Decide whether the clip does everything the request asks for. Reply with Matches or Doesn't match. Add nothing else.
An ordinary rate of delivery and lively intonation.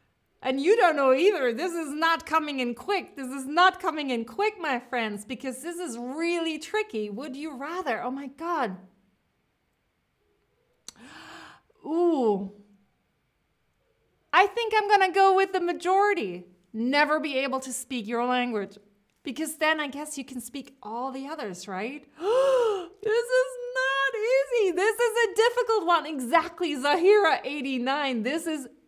Matches